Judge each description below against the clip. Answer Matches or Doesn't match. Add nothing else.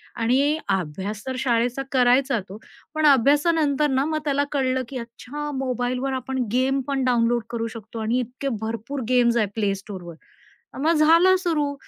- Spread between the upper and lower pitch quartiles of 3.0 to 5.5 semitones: Matches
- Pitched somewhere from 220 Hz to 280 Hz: Matches